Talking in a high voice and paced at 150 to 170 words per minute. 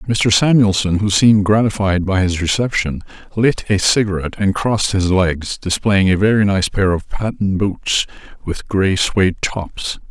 No: low, 100 Hz; average, 160 wpm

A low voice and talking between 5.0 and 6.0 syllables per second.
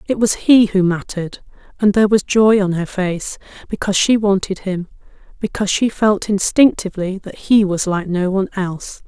No: high, 195 Hz; 5.3 syllables/s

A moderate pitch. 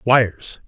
No: low, 115 Hz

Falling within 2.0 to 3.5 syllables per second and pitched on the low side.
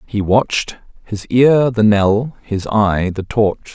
Yes: 3.4 syllables/s; low, 110 Hz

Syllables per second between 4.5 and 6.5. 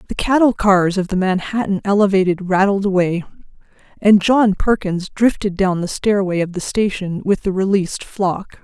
Yes: 4.9 syllables/s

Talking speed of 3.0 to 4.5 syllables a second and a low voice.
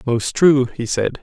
Yes: 3.6 syllables/s; low, 130 Hz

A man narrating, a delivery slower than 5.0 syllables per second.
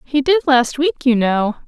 No: female; 4.1 syllables/s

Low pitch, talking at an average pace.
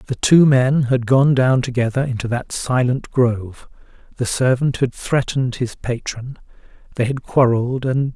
Yes: low, 125 Hz; average, 155 wpm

